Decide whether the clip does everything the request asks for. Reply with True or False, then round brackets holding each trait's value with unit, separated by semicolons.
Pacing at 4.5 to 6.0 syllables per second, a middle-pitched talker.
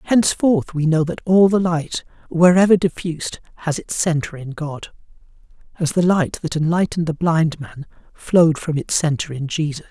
True (5.0 syllables/s; 165 Hz)